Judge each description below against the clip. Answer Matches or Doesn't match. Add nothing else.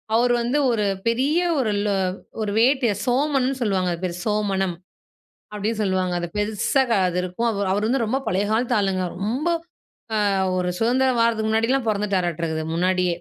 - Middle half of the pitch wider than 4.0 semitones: Matches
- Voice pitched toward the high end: Matches